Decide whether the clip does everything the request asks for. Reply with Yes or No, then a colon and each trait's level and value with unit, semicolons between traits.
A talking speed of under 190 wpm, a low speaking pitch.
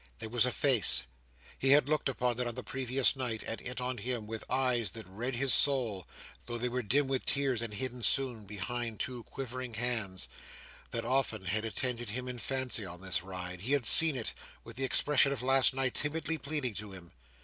No: average, 200 wpm; low, 125 Hz